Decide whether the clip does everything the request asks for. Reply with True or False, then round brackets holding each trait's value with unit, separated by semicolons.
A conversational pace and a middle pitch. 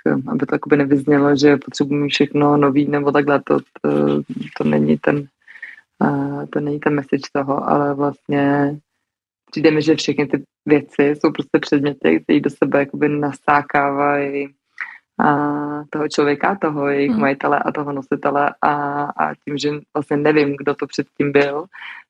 True (145 wpm; 145 Hz)